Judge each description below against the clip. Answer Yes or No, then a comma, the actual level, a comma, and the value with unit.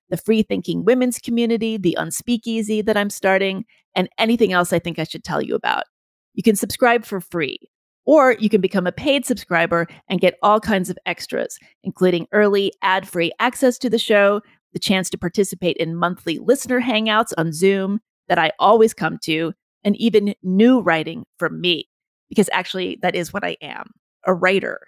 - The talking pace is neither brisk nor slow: Yes, average, 180 wpm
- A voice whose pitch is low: No, high, 200 Hz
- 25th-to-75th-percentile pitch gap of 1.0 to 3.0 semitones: No, average, 4.0 semitones